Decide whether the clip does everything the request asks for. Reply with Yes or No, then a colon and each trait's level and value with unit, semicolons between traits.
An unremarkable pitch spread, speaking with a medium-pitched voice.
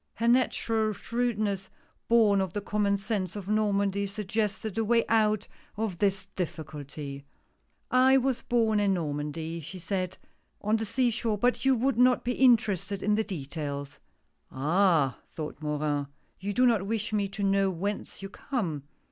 No: average, 4.2 semitones; high, 200 Hz